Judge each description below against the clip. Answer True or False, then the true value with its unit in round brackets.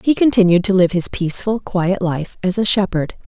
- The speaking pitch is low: False (190 Hz)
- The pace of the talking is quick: False (195 wpm)